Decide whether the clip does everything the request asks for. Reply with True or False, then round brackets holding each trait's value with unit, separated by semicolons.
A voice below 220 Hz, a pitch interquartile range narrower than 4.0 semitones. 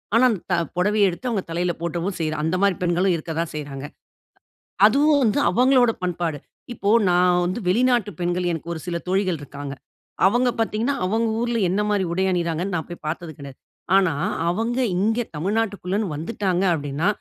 False (185 Hz; 4.3 semitones)